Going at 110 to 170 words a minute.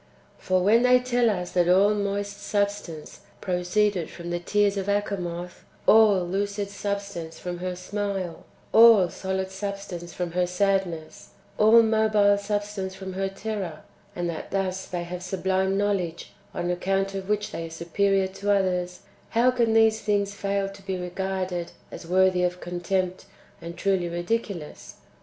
Yes: average, 160 wpm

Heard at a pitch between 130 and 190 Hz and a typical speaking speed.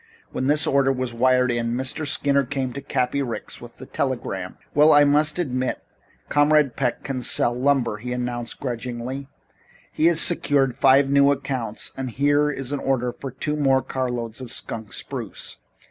Yes: low, 135 Hz; average, 170 wpm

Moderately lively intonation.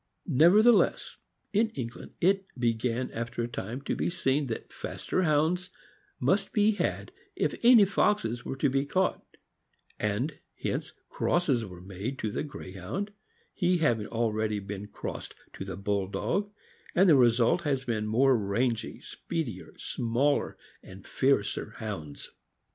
No: wide, 7.7 semitones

